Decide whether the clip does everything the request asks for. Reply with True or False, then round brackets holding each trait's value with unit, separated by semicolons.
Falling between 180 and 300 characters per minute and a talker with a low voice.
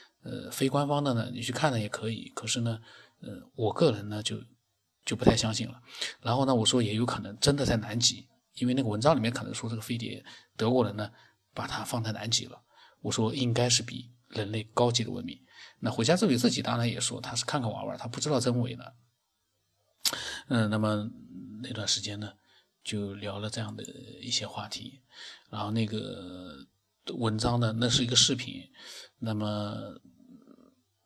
True (270 characters per minute; 120 Hz)